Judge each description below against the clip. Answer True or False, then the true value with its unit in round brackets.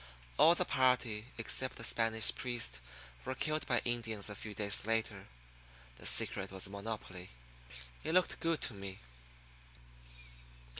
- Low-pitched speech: True (115 Hz)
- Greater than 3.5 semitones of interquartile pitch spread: True (4.1 semitones)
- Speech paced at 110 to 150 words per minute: True (140 wpm)